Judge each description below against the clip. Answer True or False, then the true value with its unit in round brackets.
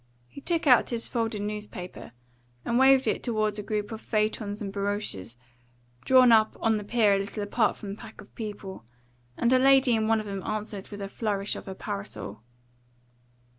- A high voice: True (215 Hz)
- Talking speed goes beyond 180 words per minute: True (190 wpm)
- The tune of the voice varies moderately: False (2.3 semitones)